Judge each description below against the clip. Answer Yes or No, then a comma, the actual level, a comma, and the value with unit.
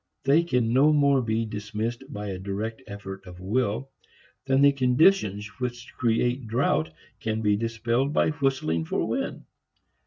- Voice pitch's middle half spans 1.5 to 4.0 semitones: No, average, 4.4 semitones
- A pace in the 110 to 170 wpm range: Yes, average, 150 wpm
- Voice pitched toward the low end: Yes, low, 115 Hz